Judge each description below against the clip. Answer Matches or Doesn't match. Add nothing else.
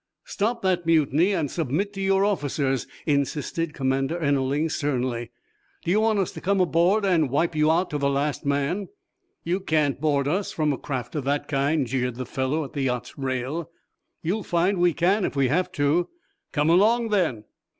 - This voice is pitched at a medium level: Matches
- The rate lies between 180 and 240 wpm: Matches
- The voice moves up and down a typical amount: Matches